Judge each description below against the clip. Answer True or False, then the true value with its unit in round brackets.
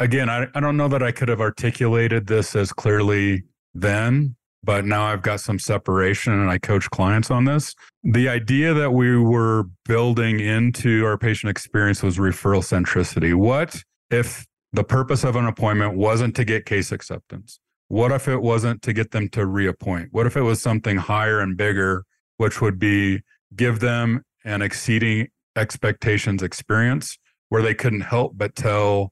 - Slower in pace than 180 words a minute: True (170 wpm)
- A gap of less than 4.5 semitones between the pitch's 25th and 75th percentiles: True (2.8 semitones)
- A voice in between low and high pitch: False (110 Hz)